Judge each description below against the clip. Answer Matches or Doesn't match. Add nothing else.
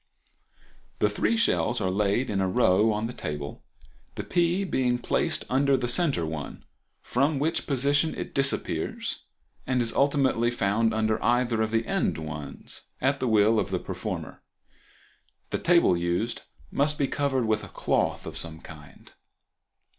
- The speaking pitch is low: Matches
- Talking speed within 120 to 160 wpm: Matches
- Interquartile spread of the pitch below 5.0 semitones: Doesn't match